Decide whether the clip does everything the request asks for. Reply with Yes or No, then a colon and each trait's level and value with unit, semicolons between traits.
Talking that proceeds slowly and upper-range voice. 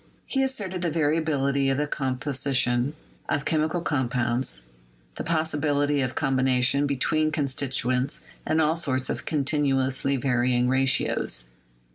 No: slow, 120 wpm; medium, 140 Hz